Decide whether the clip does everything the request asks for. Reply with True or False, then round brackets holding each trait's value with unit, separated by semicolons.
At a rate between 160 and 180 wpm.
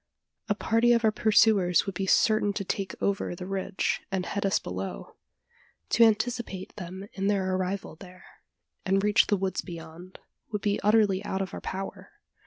True (175 wpm)